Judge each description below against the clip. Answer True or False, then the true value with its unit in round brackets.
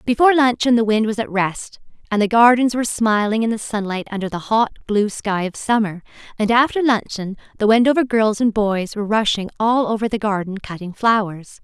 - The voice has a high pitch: True (220 Hz)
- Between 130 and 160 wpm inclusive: False (195 wpm)